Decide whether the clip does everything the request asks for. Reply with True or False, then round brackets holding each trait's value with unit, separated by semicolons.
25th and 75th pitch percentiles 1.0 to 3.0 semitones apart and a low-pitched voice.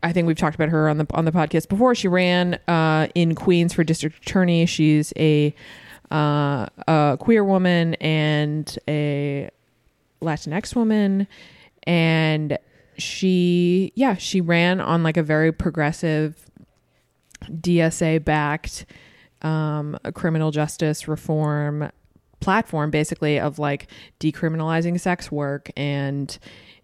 False (2.6 semitones; 155 Hz)